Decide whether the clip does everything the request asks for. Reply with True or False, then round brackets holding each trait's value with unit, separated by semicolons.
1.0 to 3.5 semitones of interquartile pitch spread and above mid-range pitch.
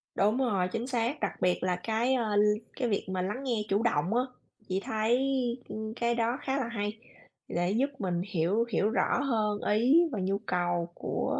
False (4.0 semitones; 215 Hz)